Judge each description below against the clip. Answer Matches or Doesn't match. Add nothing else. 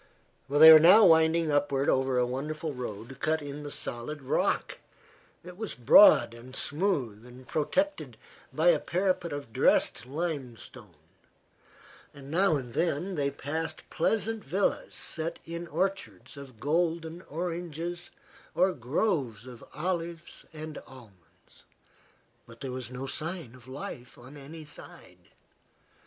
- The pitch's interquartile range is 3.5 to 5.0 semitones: Matches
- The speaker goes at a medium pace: Doesn't match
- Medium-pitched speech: Matches